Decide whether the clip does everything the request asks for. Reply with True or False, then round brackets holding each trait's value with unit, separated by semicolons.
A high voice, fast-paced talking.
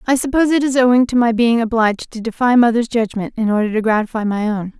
True (230 Hz; 240 wpm)